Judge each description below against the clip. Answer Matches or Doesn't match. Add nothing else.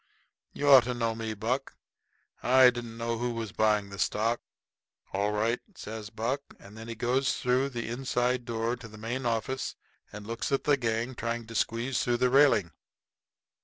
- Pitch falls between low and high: Doesn't match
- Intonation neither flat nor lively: Doesn't match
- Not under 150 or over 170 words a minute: Doesn't match